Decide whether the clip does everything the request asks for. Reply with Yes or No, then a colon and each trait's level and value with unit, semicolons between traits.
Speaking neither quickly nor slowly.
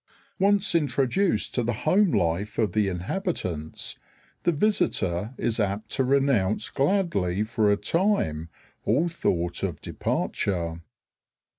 No: slow, 120 wpm